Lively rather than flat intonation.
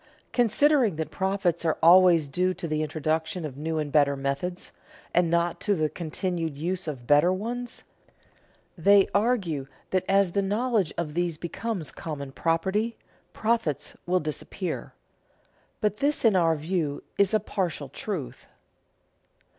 No: average, 4.3 semitones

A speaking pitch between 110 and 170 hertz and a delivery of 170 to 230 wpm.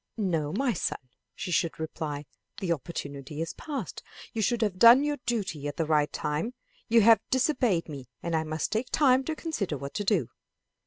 No: medium, 180 Hz; average, 190 wpm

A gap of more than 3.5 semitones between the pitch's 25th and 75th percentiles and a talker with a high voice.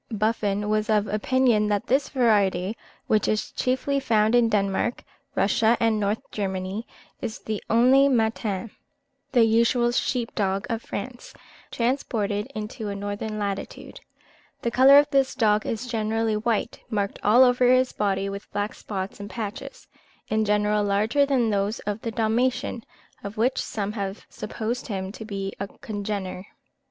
No: average, 2.8 semitones; high, 215 Hz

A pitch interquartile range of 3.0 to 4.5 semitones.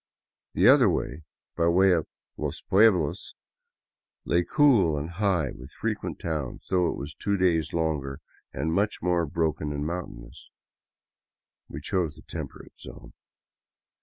Yes: average, 3.7 semitones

